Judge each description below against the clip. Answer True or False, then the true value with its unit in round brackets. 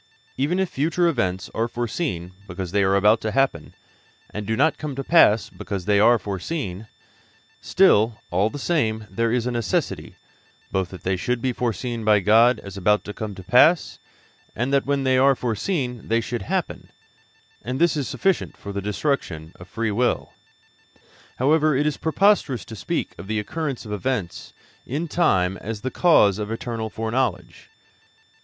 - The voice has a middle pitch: False (115 Hz)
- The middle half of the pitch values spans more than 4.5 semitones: True (5.1 semitones)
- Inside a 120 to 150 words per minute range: False (175 wpm)